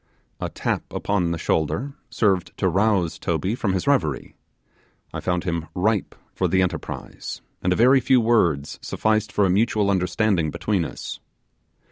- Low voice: Yes, very low, 95 Hz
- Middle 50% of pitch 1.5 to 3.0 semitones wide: No, average, 3.8 semitones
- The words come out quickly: No, average, 155 wpm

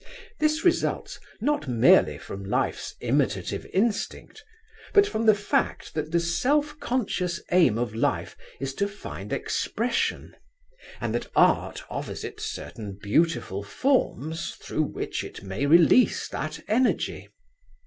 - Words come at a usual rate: No, slow, 130 wpm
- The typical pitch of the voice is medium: Yes, medium, 175 Hz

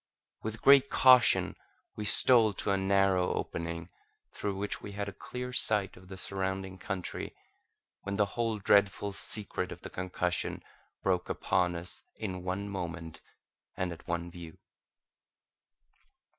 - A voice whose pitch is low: Yes, very low, 95 Hz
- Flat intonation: Yes, narrow, 2.2 semitones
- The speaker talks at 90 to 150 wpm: Yes, average, 140 wpm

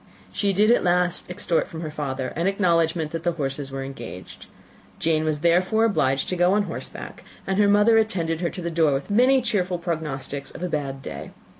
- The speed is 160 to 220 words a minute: Yes, average, 200 wpm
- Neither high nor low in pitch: Yes, medium, 170 Hz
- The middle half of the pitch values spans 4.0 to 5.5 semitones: Yes, average, 4.6 semitones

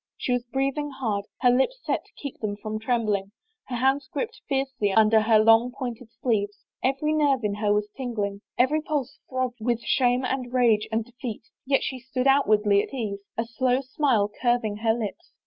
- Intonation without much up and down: No, average, 3.7 semitones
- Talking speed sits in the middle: Yes, average, 185 wpm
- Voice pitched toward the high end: Yes, high, 245 Hz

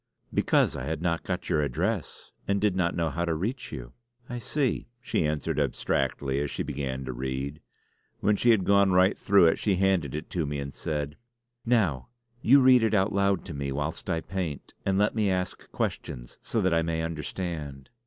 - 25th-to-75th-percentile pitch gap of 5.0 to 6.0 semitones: Yes, wide, 5.4 semitones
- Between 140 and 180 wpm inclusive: No, average, 200 wpm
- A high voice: No, very low, 85 Hz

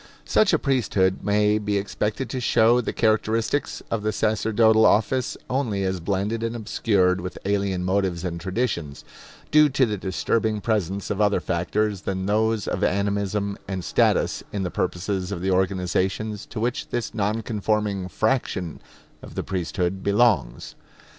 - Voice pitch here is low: Yes, low, 105 Hz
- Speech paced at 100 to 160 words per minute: Yes, average, 155 wpm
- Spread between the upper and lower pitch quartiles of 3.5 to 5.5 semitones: No, average, 2.8 semitones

